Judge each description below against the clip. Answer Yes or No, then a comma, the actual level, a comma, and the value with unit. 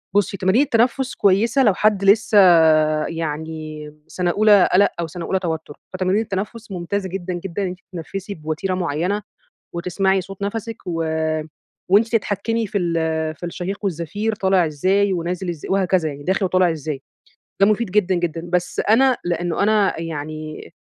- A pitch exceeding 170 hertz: Yes, medium, 185 Hz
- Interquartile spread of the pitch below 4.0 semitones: Yes, average, 3.3 semitones